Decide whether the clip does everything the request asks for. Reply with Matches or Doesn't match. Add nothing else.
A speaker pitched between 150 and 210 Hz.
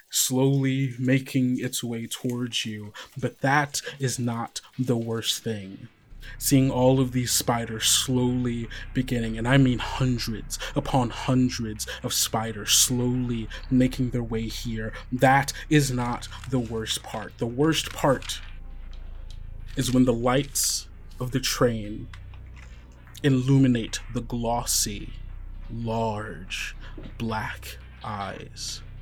Doesn't match